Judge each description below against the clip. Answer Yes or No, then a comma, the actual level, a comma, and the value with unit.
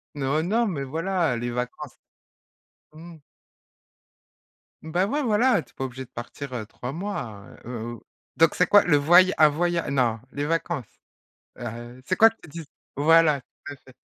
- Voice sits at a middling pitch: Yes, medium, 155 Hz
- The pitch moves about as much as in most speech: No, wide, 5.7 semitones